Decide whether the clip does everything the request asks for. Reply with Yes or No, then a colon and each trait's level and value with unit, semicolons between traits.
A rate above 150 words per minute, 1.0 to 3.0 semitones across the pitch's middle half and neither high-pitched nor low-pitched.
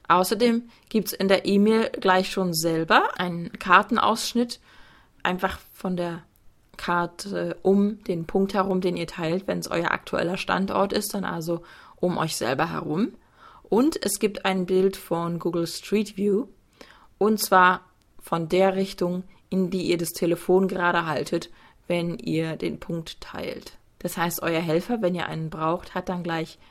Yes: average, 160 wpm; narrow, 2.5 semitones; medium, 180 Hz